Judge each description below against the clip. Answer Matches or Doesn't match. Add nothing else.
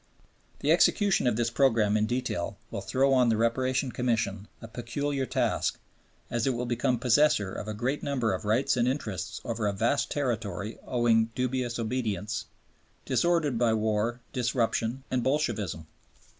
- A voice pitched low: Matches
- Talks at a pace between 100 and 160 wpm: Matches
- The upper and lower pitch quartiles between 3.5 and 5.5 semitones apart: Doesn't match